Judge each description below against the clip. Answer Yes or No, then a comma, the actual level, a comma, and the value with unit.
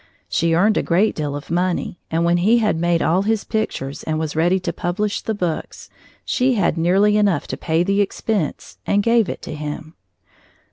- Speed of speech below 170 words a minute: No, average, 195 wpm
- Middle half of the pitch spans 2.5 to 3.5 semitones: No, average, 4.2 semitones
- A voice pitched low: No, medium, 180 Hz